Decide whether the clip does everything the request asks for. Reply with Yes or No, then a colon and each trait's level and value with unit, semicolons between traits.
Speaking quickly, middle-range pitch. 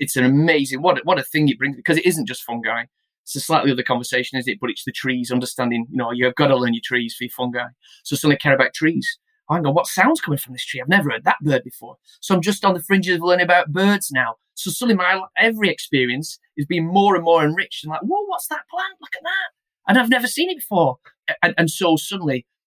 Yes: fast, 265 wpm; medium, 160 Hz